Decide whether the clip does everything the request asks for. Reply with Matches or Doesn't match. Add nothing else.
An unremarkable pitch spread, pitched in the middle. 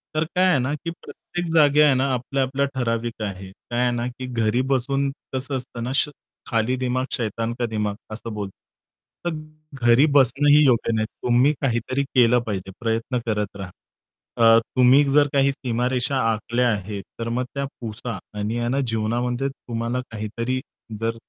Doesn't match